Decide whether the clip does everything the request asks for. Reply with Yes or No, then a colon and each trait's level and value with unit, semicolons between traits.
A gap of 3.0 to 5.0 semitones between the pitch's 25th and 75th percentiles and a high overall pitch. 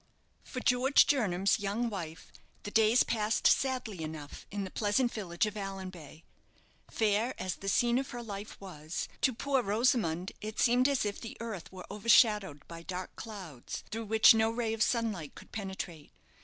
Yes: average, 3.9 semitones; high, 210 Hz